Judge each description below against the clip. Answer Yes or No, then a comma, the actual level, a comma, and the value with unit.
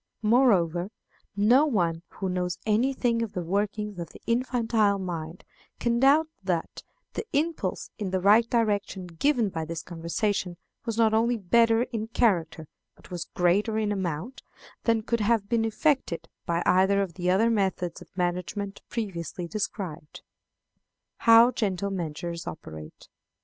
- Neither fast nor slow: Yes, average, 145 wpm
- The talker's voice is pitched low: No, high, 200 Hz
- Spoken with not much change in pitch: No, average, 4.5 semitones